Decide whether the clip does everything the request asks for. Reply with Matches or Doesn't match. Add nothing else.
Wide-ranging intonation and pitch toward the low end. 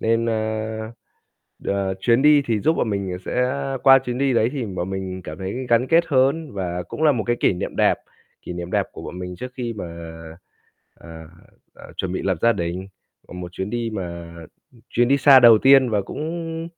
Matches